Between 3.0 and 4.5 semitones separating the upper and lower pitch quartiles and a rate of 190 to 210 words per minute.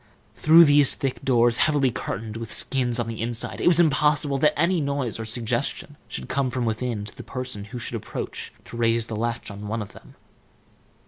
Yes: average, 3.7 semitones; average, 200 wpm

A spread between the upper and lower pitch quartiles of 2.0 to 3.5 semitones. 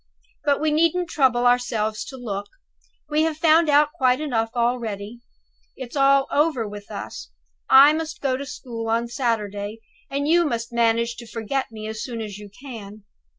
No: average, 4.4 semitones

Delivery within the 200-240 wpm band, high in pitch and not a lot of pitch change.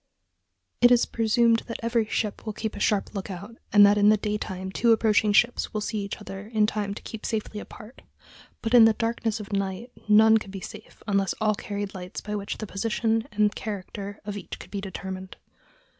Yes: fast, 205 wpm; high, 210 Hz; narrow, 1.8 semitones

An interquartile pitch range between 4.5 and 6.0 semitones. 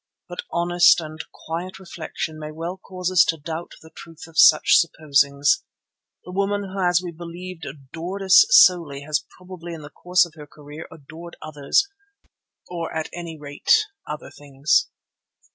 No: average, 2.8 semitones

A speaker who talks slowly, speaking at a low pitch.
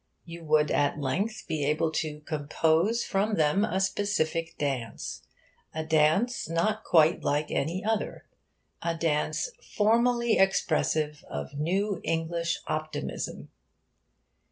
No: slow, 115 wpm; medium, 165 Hz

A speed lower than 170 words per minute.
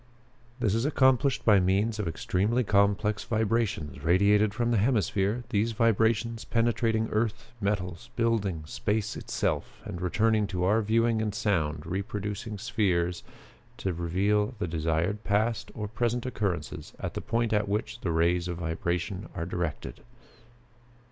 Yes: average, 140 wpm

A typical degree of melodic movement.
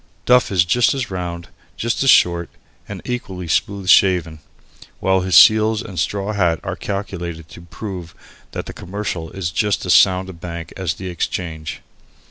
Yes: average, 3.0 semitones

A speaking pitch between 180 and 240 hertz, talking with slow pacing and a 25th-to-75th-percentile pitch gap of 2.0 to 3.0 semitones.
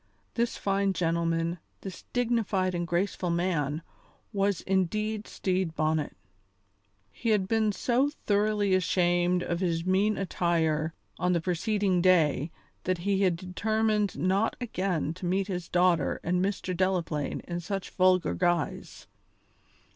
Yes: medium, 185 Hz; slow, 130 wpm; average, 2.7 semitones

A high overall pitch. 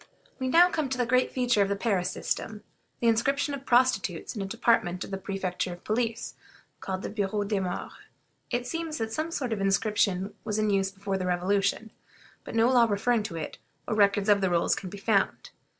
Yes: high, 210 Hz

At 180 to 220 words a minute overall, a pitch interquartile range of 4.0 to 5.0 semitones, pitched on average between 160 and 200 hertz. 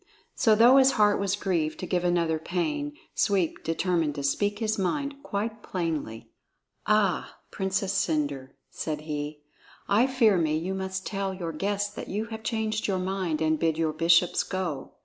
No: average, 170 wpm; average, 4.6 semitones; high, 190 Hz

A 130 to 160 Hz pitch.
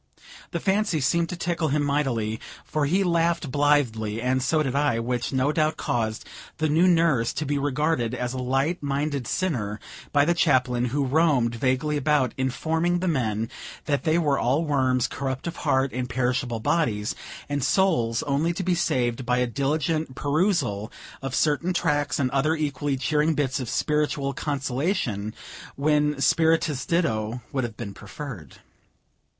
Yes: medium, 140 Hz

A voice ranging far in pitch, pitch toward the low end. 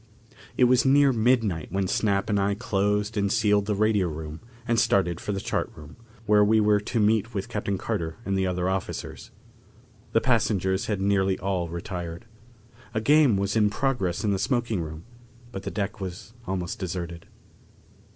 No: average, 2.9 semitones; low, 100 Hz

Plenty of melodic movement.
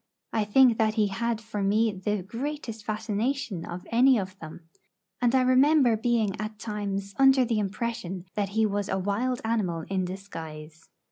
No: average, 3.3 semitones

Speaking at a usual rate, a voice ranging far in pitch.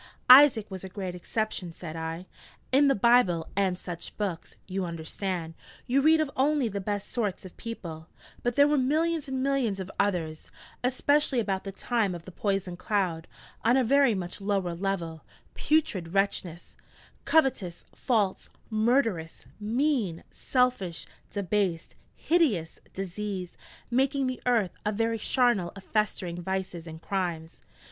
Yes: average, 145 wpm; wide, 5.9 semitones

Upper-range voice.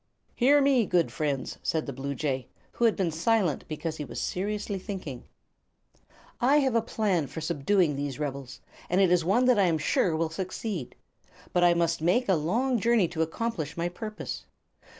No: medium, 175 Hz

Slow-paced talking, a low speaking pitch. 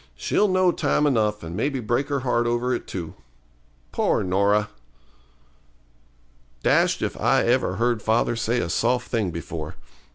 No: average, 150 wpm; low, 115 Hz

